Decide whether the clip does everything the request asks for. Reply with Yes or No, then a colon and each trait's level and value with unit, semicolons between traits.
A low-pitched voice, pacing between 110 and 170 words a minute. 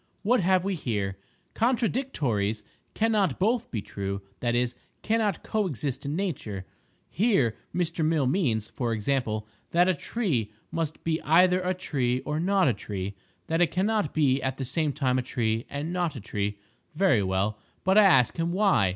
No: medium, 150 Hz; average, 165 wpm